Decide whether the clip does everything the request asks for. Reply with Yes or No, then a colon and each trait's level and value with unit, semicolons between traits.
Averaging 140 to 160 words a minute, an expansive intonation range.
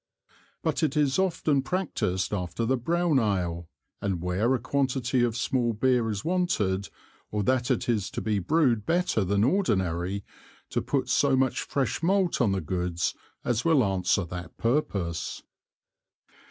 Yes: average, 155 wpm; wide, 6.4 semitones